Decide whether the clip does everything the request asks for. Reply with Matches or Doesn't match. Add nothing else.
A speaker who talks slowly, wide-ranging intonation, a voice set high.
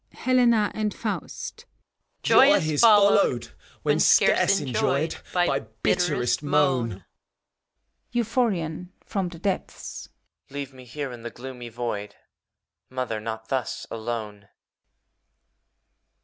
Doesn't match